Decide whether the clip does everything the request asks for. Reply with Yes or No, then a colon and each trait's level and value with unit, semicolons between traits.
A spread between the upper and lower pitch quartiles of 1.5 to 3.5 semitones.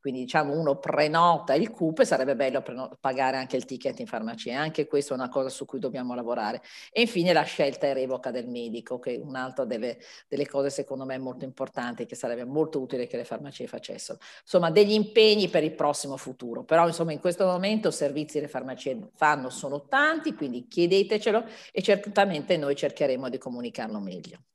No: average, 4.7 semitones